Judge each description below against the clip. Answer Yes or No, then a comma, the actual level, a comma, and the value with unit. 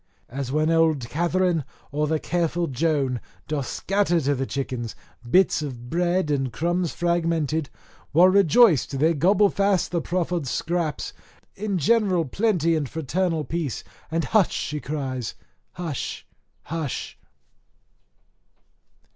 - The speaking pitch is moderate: Yes, medium, 160 Hz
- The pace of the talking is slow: Yes, slow, 120 wpm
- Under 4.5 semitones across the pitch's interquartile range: Yes, average, 3.7 semitones